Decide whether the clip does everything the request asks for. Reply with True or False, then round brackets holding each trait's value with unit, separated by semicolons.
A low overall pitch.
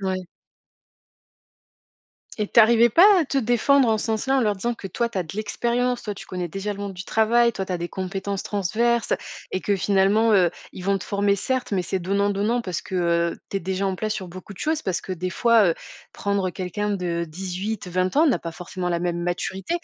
False (200 Hz)